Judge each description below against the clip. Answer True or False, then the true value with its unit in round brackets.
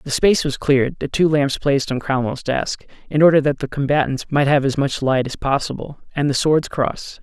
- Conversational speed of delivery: False (225 wpm)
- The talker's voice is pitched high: False (140 Hz)